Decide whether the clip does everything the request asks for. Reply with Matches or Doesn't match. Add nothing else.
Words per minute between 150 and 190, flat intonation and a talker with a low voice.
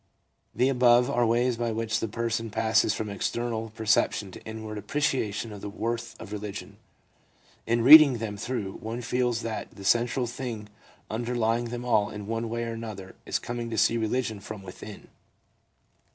Matches